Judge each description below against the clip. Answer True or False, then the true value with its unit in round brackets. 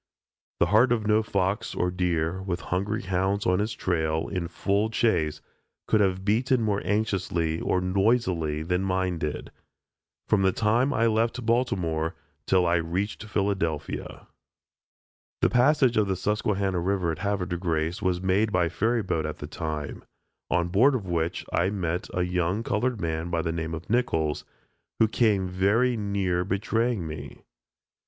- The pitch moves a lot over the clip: False (3.8 semitones)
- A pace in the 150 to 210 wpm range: True (160 wpm)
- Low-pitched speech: True (95 Hz)